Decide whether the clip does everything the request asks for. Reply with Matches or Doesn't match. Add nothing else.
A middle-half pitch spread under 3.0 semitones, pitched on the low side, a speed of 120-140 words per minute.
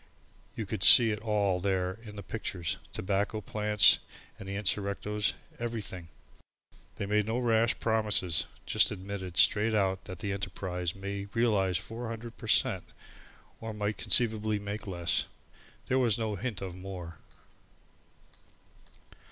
Matches